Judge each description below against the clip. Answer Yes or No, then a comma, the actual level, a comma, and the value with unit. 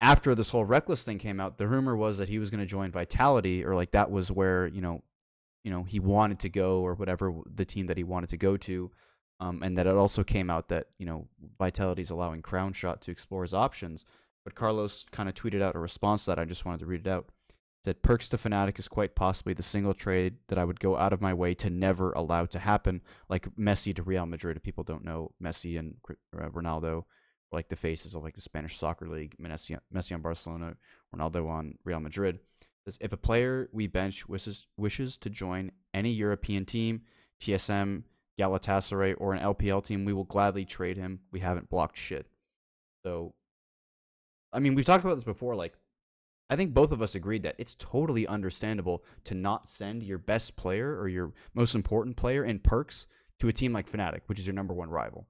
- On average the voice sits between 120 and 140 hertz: No, very low, 95 Hz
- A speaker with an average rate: No, fast, 215 wpm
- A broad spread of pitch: No, average, 2.9 semitones